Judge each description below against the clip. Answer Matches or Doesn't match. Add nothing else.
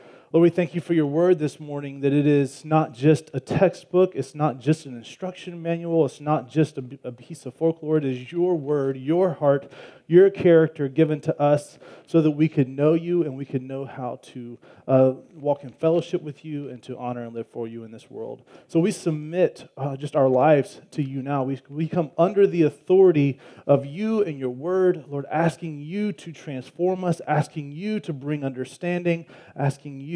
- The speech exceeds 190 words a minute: Matches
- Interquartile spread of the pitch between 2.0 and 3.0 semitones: Doesn't match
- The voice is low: Doesn't match